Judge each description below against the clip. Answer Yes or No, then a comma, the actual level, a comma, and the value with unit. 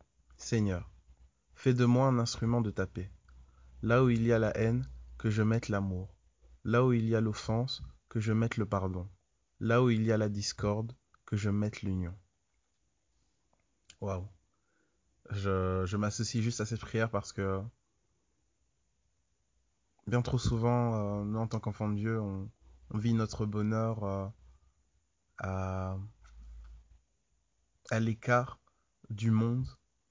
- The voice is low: Yes, low, 100 Hz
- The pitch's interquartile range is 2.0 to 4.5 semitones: No, wide, 5.4 semitones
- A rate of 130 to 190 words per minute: Yes, slow, 145 wpm